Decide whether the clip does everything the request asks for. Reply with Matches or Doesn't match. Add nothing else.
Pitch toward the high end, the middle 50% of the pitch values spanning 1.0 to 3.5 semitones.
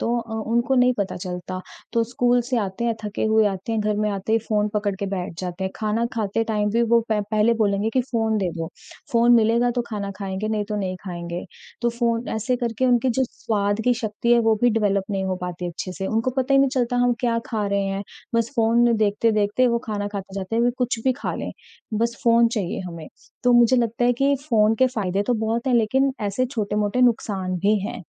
Matches